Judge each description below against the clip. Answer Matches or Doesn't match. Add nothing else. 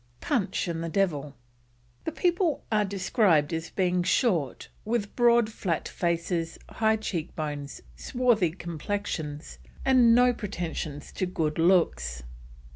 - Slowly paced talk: Matches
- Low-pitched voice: Doesn't match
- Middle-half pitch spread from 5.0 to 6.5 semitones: Matches